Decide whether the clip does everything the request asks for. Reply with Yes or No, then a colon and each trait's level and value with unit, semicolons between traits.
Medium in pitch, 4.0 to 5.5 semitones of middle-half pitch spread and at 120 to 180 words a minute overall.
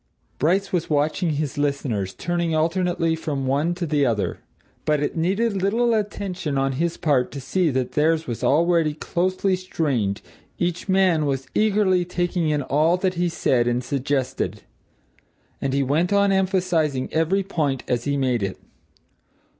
Yes: medium, 160 Hz; average, 4.8 semitones; average, 155 wpm